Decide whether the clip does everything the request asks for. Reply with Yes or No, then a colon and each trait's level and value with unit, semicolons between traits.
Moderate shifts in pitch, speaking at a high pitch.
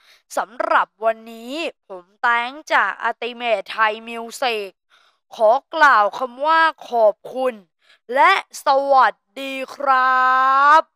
Yes: average, 3.7 semitones; very high, 255 Hz